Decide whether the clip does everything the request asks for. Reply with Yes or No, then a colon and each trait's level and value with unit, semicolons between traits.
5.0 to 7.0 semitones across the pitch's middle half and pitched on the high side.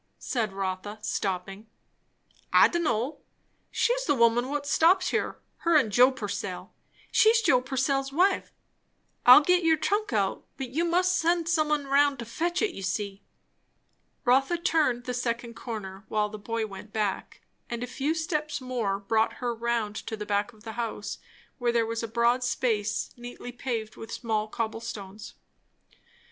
Yes: average, 5.3 semitones; high, 240 Hz